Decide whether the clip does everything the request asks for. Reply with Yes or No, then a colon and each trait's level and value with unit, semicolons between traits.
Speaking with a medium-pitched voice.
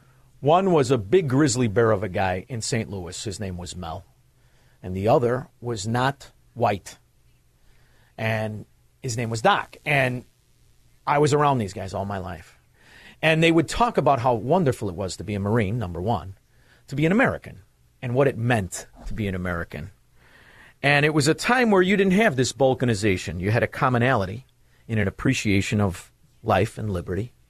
No: low, 120 Hz